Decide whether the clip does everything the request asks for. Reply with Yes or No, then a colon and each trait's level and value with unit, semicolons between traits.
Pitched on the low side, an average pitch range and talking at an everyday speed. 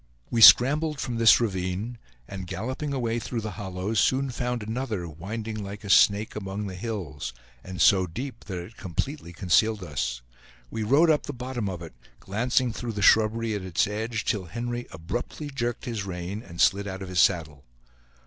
Yes: low, 105 Hz; average, 4.4 semitones; average, 180 wpm